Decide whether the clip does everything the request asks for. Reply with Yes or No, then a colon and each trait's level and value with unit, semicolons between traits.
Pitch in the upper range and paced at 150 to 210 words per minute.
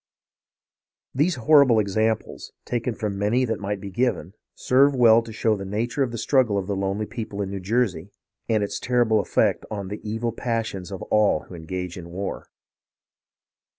No: low, 110 Hz; average, 175 wpm